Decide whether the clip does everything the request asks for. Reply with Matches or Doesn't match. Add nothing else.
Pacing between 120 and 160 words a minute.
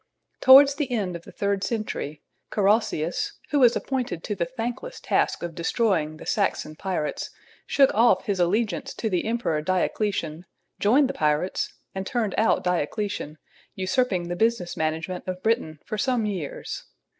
Matches